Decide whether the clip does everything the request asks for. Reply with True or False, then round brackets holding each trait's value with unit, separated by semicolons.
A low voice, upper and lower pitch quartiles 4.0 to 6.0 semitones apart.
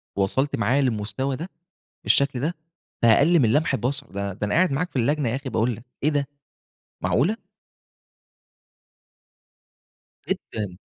True (130 Hz; 4.7 semitones)